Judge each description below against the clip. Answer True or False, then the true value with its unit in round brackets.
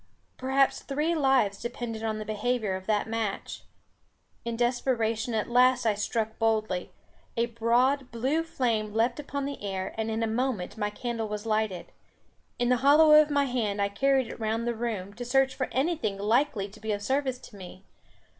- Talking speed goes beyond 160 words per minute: True (185 wpm)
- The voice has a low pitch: False (230 Hz)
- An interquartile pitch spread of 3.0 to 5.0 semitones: True (3.5 semitones)